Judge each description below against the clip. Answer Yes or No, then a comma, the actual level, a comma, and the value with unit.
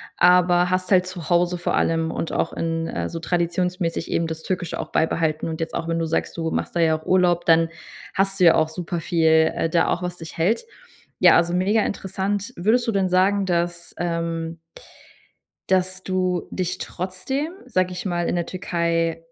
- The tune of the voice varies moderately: No, narrow, 1.8 semitones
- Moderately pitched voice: Yes, medium, 175 Hz